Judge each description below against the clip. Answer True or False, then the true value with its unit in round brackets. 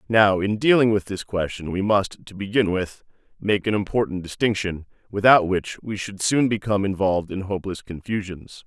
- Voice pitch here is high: False (100 Hz)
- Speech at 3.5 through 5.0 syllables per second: False (5.2 syllables/s)